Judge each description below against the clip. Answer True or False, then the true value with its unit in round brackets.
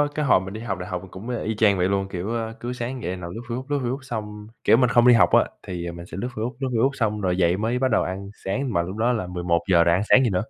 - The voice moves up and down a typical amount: True (4.8 semitones)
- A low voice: True (105 Hz)